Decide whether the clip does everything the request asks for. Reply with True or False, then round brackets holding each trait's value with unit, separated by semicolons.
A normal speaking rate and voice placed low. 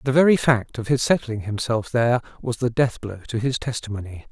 False (210 wpm; 120 Hz)